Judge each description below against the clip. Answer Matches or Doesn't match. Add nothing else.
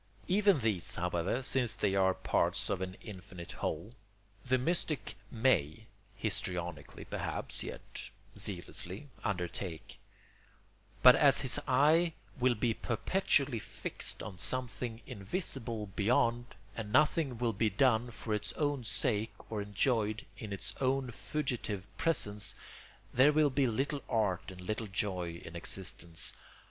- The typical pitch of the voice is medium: Doesn't match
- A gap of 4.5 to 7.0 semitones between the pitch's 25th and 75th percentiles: Matches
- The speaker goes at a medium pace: Doesn't match